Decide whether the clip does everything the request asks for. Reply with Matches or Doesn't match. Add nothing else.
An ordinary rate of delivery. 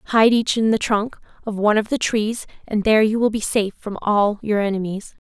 Doesn't match